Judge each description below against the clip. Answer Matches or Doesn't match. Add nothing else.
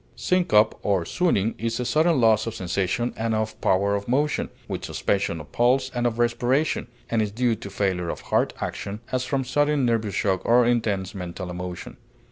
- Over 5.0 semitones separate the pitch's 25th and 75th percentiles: Doesn't match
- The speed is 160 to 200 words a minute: Matches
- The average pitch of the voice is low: Matches